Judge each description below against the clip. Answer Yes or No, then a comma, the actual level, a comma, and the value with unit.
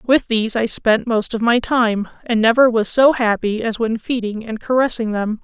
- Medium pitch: No, high, 230 Hz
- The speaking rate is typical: No, fast, 210 wpm